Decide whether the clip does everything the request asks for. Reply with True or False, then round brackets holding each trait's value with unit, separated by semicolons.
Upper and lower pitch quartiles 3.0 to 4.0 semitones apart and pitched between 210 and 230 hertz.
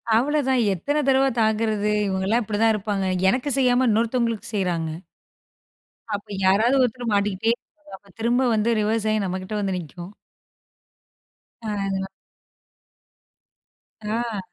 True (3.7 semitones; 220 Hz)